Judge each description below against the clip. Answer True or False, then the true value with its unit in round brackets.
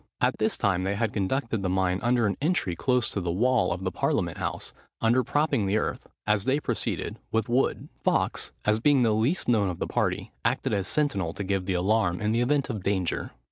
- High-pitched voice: False (105 Hz)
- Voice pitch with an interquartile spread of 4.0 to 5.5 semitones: True (4.5 semitones)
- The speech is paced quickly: True (220 wpm)